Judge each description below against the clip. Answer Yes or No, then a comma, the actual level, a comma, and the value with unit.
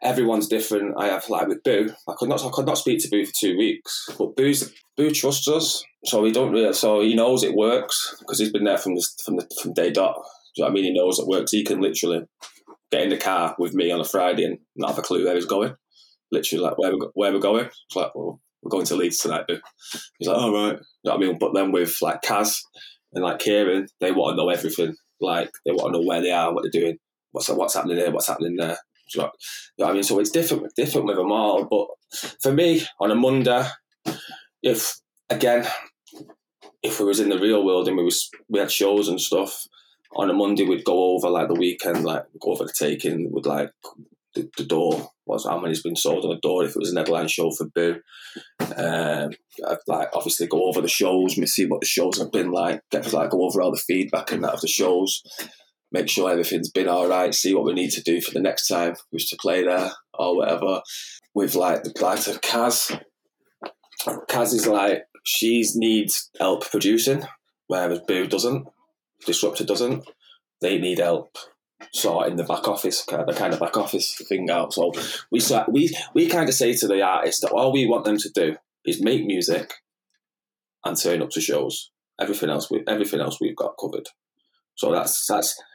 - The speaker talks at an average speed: No, fast, 225 wpm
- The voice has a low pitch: Yes, low, 105 Hz